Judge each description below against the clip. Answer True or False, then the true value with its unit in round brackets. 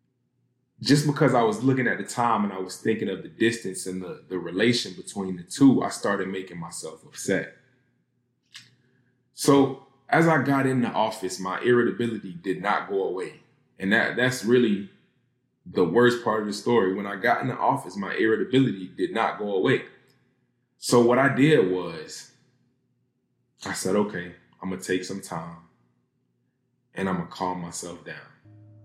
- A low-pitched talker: True (110 Hz)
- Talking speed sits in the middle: True (175 wpm)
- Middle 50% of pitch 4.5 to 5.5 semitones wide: True (5.2 semitones)